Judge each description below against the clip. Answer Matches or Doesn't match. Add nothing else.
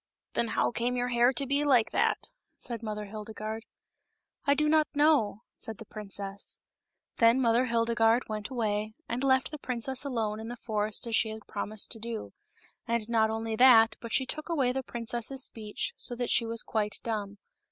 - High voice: Matches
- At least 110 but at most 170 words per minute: Doesn't match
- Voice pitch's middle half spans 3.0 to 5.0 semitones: Doesn't match